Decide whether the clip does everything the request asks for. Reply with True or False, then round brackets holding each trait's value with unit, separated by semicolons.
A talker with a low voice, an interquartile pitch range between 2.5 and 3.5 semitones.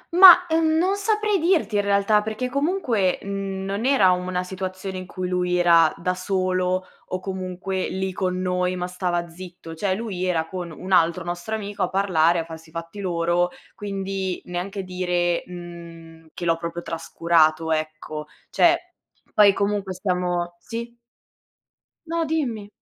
False (185 Hz; 2.8 semitones)